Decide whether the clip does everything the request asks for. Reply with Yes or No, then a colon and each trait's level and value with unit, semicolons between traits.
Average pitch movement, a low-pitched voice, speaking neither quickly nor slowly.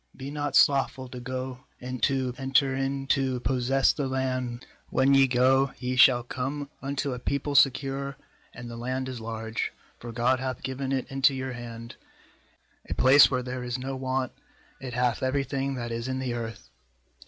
No: narrow, 1.6 semitones; low, 130 Hz; average, 180 wpm